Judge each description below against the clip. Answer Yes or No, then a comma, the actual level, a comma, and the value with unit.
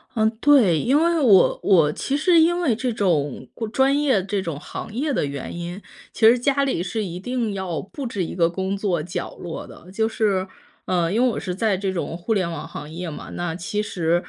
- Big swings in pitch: Yes, wide, 5.8 semitones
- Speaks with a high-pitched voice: Yes, high, 195 Hz